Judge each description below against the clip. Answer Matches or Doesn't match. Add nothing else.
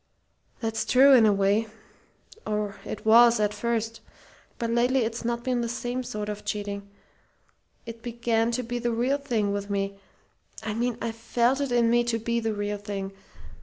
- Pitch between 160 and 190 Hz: Doesn't match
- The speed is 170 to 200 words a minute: Matches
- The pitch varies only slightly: Matches